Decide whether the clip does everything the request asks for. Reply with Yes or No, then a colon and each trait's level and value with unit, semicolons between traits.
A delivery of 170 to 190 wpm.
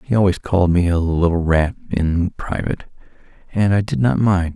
Yes: average, 185 wpm